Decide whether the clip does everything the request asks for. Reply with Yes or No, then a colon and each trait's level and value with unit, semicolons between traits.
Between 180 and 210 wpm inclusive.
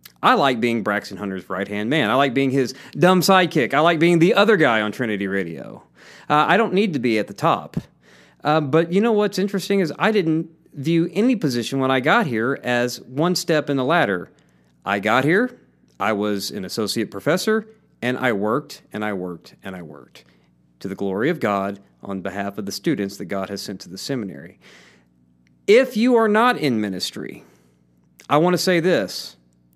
Yes: average, 200 wpm